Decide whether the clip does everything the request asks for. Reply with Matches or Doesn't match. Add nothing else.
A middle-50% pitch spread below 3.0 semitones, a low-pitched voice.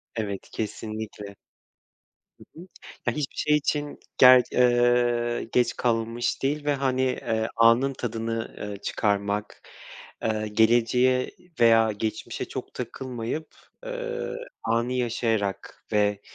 Matches